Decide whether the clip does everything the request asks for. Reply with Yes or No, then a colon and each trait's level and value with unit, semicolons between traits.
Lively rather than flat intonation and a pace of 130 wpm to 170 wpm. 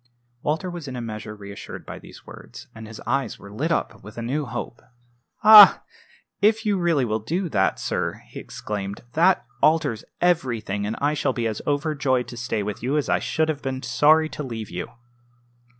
No: wide, 6.2 semitones; average, 195 wpm